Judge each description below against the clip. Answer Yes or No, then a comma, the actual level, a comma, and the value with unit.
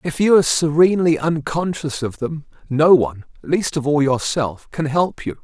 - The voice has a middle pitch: Yes, medium, 150 Hz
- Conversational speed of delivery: Yes, average, 155 wpm